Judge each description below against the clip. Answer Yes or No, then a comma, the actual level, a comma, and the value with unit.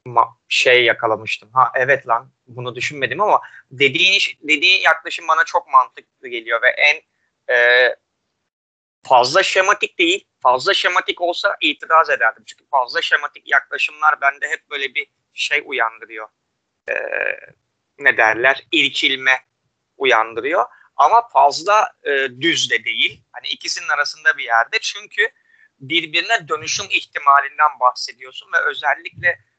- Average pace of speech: Yes, average, 120 wpm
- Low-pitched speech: No, medium, 170 Hz